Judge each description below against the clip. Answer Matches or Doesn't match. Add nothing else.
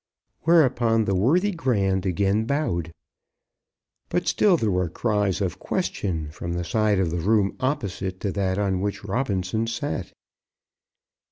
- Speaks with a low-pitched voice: Matches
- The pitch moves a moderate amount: Matches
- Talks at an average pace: Matches